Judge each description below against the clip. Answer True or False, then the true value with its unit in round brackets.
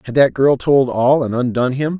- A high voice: False (130 Hz)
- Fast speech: True (240 wpm)